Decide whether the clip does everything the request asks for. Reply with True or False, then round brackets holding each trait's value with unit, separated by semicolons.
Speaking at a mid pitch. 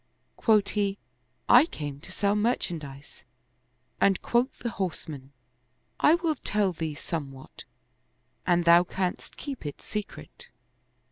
True (180 Hz)